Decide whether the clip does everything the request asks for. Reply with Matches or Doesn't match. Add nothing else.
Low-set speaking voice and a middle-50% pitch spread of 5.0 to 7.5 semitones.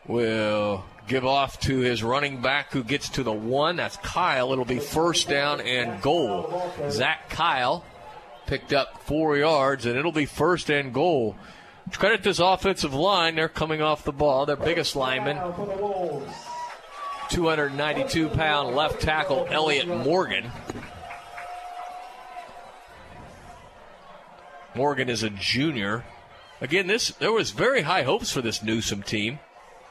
Doesn't match